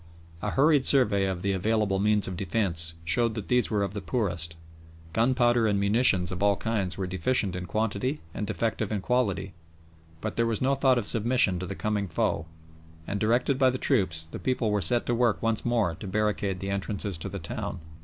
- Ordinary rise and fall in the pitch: Yes, average, 3.9 semitones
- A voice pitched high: No, low, 105 Hz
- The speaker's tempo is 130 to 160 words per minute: No, fast, 205 wpm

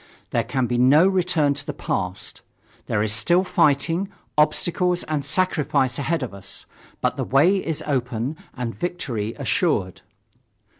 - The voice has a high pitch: No, medium, 145 Hz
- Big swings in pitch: Yes, wide, 6.0 semitones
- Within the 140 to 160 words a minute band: Yes, average, 145 wpm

